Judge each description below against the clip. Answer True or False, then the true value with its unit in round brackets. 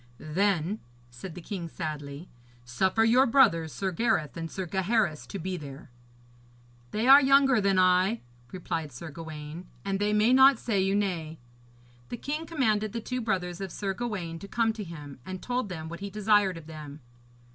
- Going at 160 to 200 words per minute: True (180 wpm)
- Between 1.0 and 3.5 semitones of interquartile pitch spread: False (5.1 semitones)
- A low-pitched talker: False (190 Hz)